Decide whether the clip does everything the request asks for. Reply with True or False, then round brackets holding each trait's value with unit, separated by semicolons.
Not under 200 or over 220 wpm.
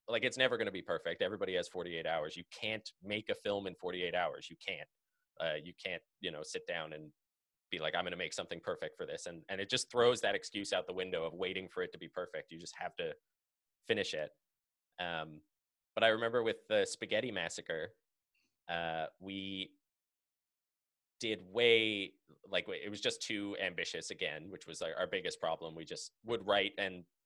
True (205 wpm)